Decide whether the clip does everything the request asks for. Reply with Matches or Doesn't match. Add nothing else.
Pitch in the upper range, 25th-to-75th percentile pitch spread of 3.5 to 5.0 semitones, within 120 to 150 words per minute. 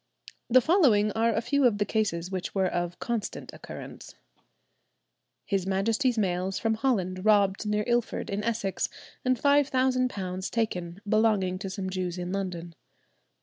Matches